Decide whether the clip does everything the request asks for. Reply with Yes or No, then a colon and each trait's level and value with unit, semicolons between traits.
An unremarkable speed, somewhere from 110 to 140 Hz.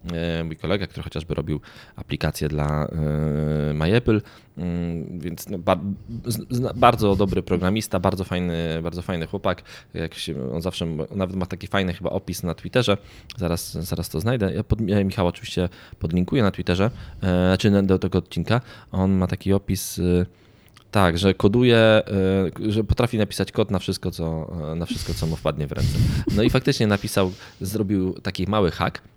No: average, 150 wpm; very low, 95 Hz